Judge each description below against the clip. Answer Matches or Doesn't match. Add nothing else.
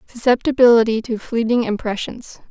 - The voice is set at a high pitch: Matches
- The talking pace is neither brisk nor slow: Doesn't match